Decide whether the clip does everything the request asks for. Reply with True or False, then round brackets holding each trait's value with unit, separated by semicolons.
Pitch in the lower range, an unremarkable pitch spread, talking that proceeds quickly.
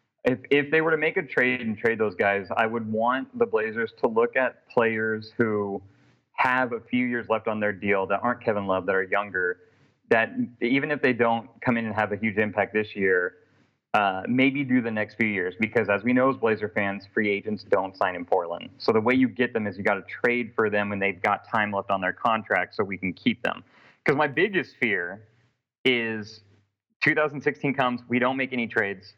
True (115 Hz; 3.4 semitones; 225 wpm)